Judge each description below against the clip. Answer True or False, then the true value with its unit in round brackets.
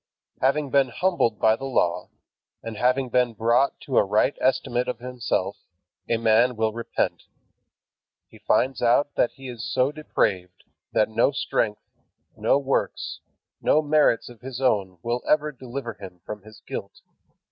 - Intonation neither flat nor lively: True (3.4 semitones)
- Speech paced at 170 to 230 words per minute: False (155 wpm)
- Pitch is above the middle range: False (120 Hz)